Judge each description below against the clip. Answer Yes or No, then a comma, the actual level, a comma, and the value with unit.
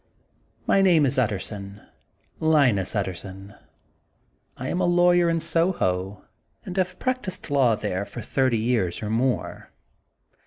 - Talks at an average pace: No, slow, 130 wpm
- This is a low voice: Yes, low, 130 Hz